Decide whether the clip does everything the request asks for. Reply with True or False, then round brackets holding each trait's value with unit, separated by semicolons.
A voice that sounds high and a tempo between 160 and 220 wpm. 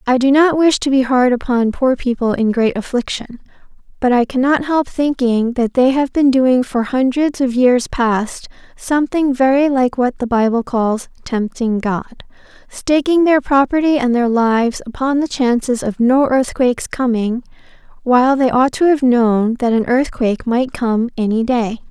True (250 Hz; 170 wpm)